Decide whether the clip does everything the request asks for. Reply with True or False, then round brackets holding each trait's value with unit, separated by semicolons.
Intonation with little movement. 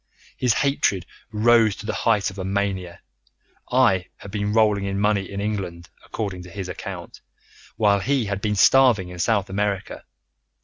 True (2.3 semitones)